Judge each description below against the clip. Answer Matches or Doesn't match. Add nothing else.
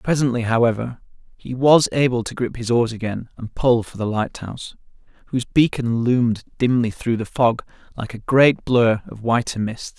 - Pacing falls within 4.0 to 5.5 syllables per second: Matches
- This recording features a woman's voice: Doesn't match